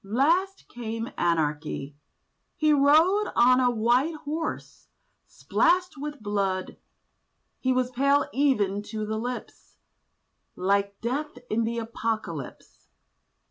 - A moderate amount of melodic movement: No, wide, 5.8 semitones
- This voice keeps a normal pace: No, slow, 105 wpm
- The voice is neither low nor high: No, high, 240 Hz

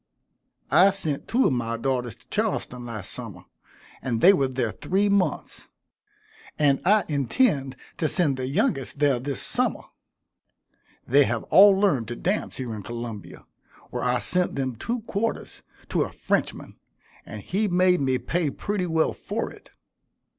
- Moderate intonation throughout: No, wide, 7.0 semitones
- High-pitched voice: No, medium, 140 Hz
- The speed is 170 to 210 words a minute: No, average, 155 wpm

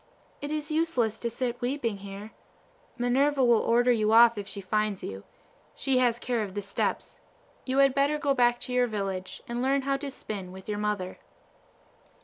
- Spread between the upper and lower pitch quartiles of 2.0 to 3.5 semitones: No, average, 4.1 semitones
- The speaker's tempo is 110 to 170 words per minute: No, average, 185 wpm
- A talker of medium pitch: No, high, 235 Hz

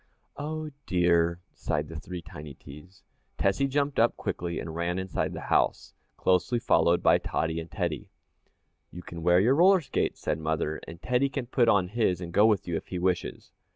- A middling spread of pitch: No, wide, 6.0 semitones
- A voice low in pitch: Yes, very low, 90 Hz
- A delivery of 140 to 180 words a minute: No, average, 190 wpm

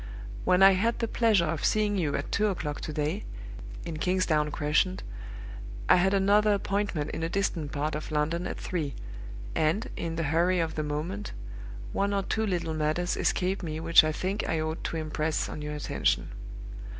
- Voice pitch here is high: No, medium, 170 Hz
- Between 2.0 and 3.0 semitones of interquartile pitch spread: No, average, 4.0 semitones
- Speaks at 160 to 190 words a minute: Yes, average, 185 wpm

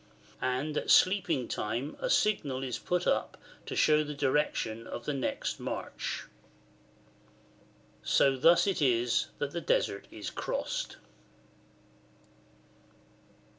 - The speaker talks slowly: Yes, slow, 115 wpm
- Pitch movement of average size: Yes, average, 4.3 semitones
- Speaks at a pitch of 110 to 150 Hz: Yes, medium, 140 Hz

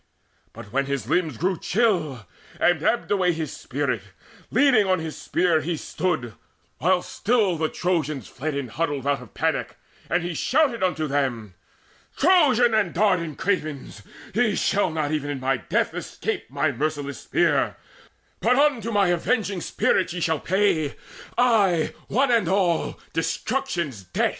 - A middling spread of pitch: No, wide, 6.0 semitones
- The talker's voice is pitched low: No, medium, 175 Hz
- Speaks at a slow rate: No, average, 150 wpm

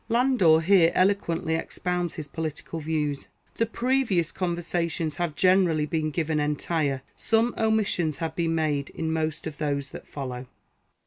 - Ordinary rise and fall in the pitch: Yes, average, 3.1 semitones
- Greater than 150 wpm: No, average, 145 wpm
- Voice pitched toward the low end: No, medium, 165 Hz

